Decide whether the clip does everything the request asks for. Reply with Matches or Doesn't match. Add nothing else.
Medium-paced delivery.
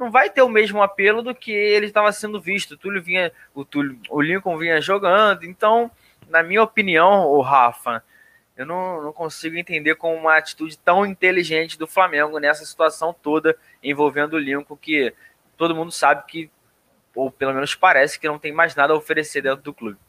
Doesn't match